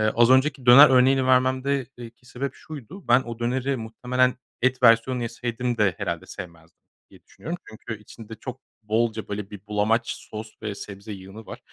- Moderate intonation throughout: Yes, average, 3.2 semitones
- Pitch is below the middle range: Yes, low, 120 Hz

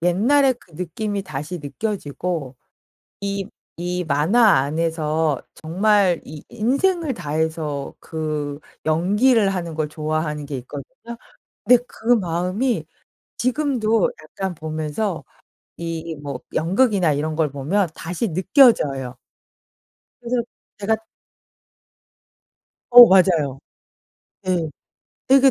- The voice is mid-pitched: Yes, medium, 170 Hz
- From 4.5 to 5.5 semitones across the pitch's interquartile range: No, wide, 6.0 semitones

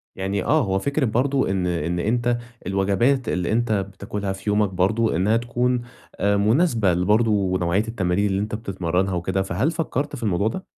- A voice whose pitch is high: No, low, 100 Hz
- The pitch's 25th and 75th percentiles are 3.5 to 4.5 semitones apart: Yes, average, 3.8 semitones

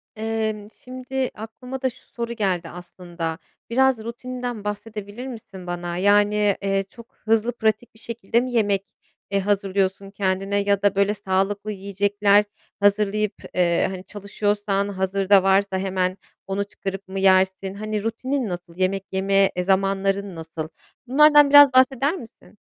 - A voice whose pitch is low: No, high, 200 Hz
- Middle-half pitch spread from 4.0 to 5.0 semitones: No, narrow, 2.6 semitones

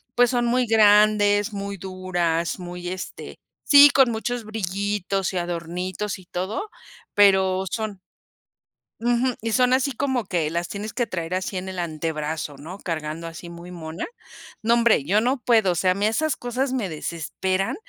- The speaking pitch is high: Yes, high, 195 Hz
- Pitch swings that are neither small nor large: Yes, average, 4.5 semitones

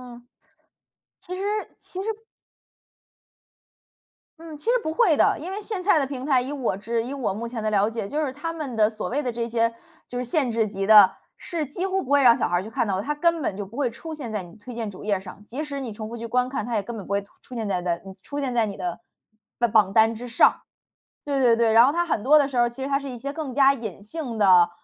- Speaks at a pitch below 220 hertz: No, high, 240 Hz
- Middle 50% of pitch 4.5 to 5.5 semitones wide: Yes, average, 4.9 semitones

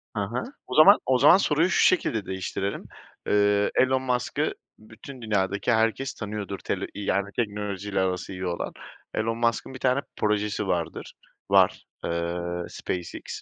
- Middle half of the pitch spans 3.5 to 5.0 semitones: Yes, average, 4.5 semitones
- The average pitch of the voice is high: No, low, 105 Hz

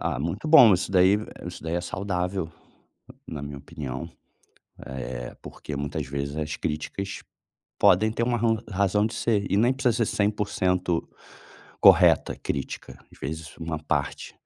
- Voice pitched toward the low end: Yes, very low, 90 Hz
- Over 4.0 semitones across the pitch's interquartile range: Yes, wide, 5.5 semitones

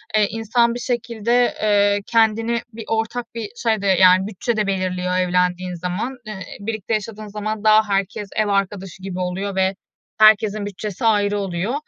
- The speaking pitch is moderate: No, high, 205 Hz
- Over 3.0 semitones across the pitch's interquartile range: No, narrow, 2.6 semitones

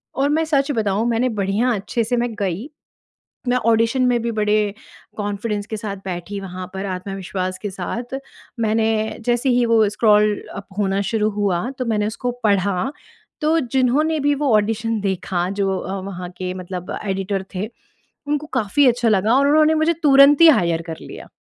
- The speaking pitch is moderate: No, high, 215 Hz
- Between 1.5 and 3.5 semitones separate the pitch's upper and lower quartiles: No, average, 4.2 semitones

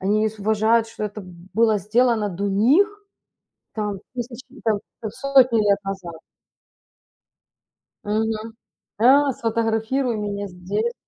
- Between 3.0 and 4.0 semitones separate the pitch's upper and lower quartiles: No, narrow, 2.4 semitones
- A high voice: Yes, high, 220 Hz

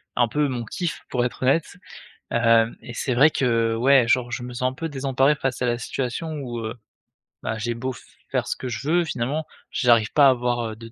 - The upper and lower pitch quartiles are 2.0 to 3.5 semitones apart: Yes, narrow, 2.6 semitones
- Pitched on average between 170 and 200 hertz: No, low, 125 Hz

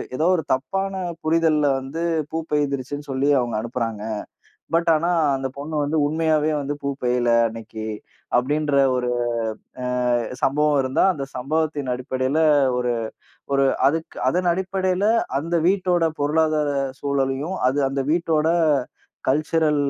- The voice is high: No, medium, 145 Hz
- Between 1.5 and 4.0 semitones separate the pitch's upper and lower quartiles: Yes, average, 3.3 semitones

